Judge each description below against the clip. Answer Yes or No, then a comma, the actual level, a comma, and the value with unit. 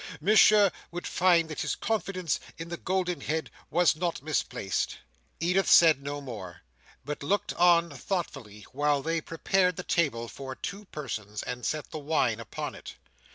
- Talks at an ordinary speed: Yes, average, 155 wpm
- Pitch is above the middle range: No, medium, 160 Hz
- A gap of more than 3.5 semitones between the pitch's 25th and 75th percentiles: Yes, average, 4.7 semitones